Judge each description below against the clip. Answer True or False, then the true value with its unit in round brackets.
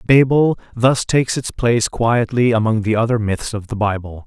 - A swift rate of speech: False (185 wpm)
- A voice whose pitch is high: False (115 Hz)